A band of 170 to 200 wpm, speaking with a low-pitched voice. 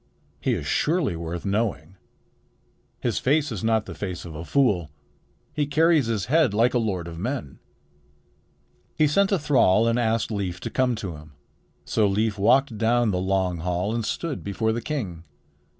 Yes: average, 175 wpm; low, 110 Hz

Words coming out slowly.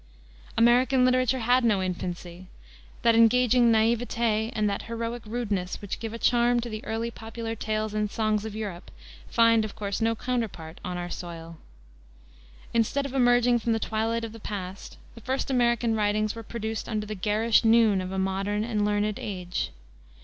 No: average, 170 wpm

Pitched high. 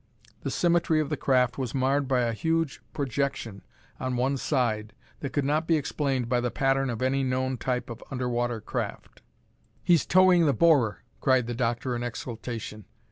No: low, 130 Hz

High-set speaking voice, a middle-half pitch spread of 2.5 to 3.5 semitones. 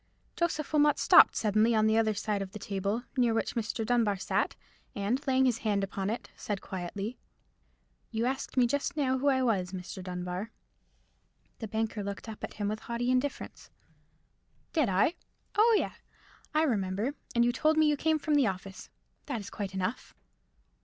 No: high, 225 Hz; average, 4.7 semitones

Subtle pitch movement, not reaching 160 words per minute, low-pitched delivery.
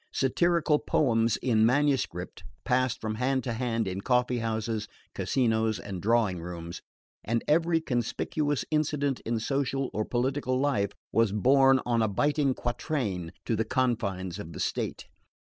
No: average, 3.9 semitones; average, 145 wpm; low, 120 Hz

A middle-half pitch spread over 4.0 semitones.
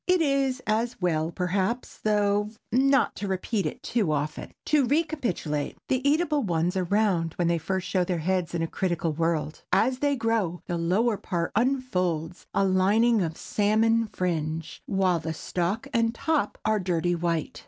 Yes: wide, 5.4 semitones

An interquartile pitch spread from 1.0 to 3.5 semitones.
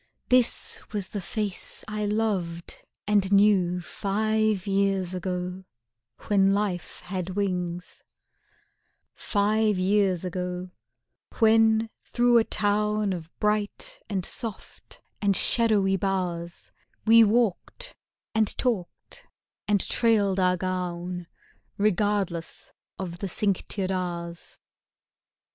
Yes: average, 2.8 semitones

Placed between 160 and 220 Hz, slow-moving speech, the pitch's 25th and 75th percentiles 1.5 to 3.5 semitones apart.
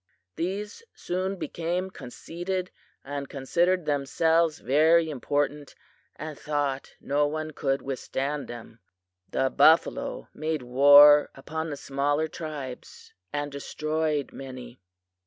No: medium, 150 Hz; slow, 105 wpm; average, 2.7 semitones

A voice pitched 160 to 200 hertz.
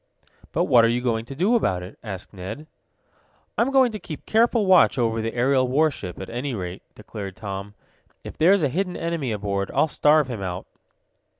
No: low, 125 Hz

